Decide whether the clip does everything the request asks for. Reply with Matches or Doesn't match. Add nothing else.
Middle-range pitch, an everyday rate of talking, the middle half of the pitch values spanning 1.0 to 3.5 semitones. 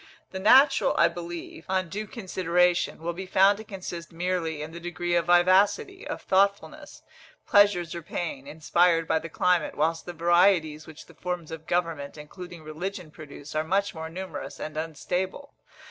Matches